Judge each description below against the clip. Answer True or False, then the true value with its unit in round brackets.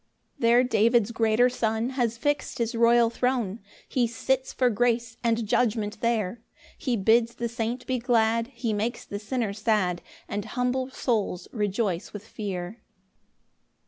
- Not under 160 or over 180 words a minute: False (145 wpm)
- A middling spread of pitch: False (2.2 semitones)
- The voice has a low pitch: False (230 Hz)